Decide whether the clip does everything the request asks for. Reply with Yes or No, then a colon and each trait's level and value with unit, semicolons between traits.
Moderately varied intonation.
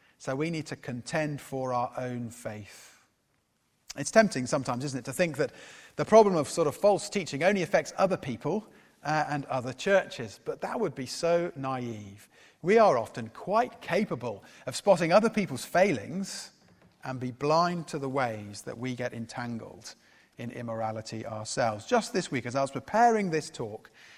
No: wide, 6.3 semitones